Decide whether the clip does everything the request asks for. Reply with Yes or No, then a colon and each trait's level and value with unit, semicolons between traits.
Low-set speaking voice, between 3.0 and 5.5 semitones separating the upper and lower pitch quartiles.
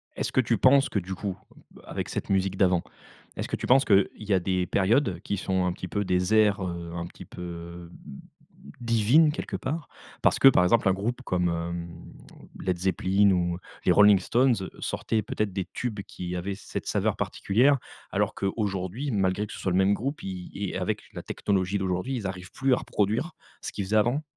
Yes: very low, 95 Hz; average, 3.4 semitones